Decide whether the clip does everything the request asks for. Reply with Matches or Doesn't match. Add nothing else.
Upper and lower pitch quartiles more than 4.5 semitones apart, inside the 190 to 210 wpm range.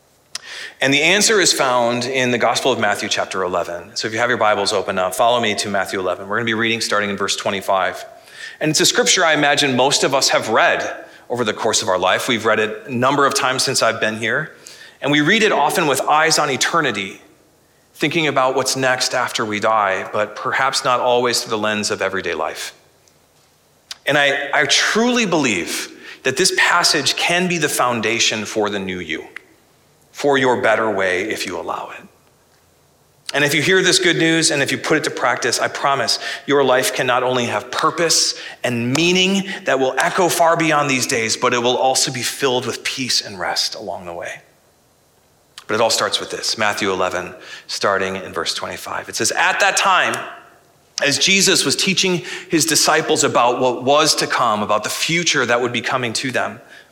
Matches